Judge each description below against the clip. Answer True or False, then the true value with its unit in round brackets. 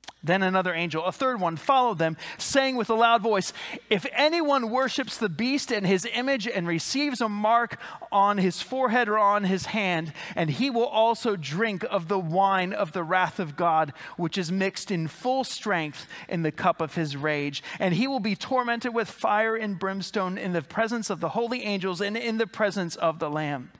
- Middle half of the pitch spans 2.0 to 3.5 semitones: False (5.0 semitones)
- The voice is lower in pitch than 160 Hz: False (205 Hz)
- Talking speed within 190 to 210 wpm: True (200 wpm)